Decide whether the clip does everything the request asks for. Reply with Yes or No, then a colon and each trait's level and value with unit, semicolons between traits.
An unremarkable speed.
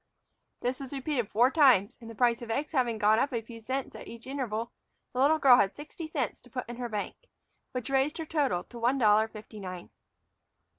No: fast, 215 wpm